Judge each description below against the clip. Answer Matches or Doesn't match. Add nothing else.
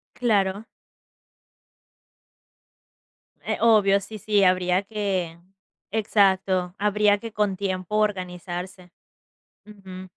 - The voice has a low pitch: Doesn't match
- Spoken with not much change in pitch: Matches